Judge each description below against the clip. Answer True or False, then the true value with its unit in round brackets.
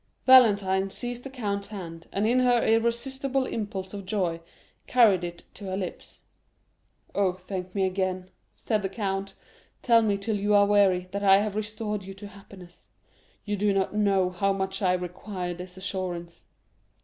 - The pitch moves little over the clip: True (2.3 semitones)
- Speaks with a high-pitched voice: True (200 Hz)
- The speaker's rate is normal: True (170 wpm)